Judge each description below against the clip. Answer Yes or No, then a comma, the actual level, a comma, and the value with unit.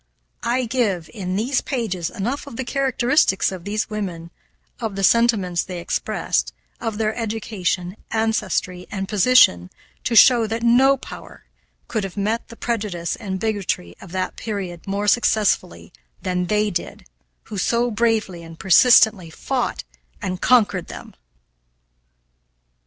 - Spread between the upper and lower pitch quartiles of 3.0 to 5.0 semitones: Yes, average, 4.1 semitones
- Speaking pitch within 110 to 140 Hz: No, high, 210 Hz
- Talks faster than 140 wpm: No, slow, 135 wpm